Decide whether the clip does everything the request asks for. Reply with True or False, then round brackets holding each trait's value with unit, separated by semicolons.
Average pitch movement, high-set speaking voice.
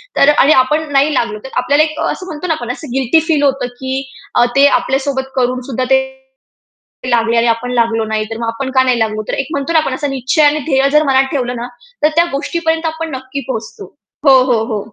True (3.4 semitones; 265 Hz)